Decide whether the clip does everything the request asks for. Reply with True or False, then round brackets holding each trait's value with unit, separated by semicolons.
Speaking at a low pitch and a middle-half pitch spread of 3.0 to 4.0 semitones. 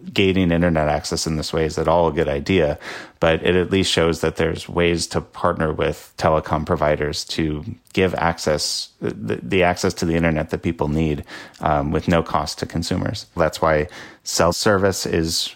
False (85 Hz; 2.4 semitones)